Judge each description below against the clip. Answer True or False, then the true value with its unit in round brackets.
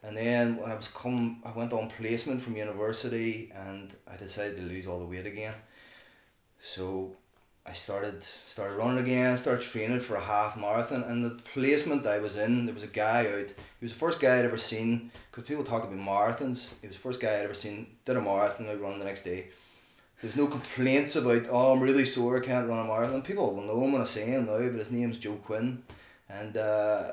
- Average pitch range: True (3.2 semitones)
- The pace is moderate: False (225 wpm)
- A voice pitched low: True (115 Hz)